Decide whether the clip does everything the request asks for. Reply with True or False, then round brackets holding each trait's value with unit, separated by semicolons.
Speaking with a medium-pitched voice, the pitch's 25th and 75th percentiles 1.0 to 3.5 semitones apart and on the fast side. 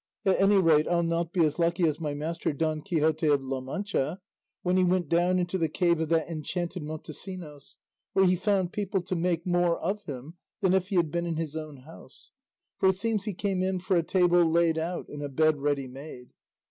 True (170 Hz; 2.9 semitones; 220 wpm)